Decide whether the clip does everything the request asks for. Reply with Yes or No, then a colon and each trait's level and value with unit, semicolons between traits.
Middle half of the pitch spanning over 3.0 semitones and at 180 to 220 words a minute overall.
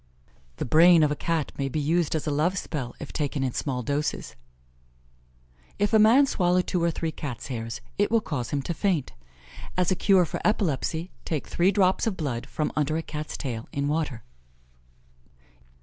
Yes: average, 4.2 semitones; average, 185 wpm